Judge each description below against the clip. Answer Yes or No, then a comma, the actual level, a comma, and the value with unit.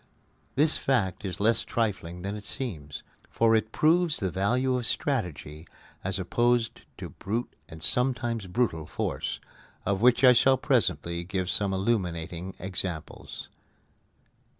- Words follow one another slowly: Yes, slow, 130 wpm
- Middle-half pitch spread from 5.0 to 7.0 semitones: Yes, average, 5.3 semitones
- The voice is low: Yes, low, 100 Hz